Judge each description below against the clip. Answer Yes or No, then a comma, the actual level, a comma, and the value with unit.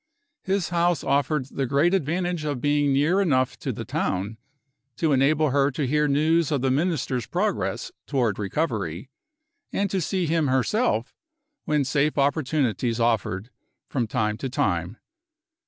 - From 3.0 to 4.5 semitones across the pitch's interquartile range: Yes, average, 4.1 semitones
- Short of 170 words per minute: Yes, average, 145 wpm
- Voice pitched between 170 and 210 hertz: No, medium, 140 Hz